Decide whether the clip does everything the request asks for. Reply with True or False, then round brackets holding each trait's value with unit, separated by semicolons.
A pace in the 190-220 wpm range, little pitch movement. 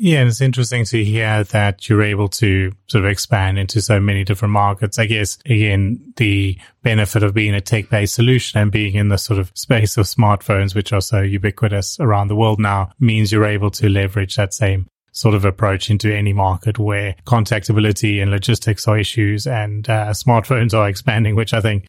True (200 wpm; 1.8 semitones)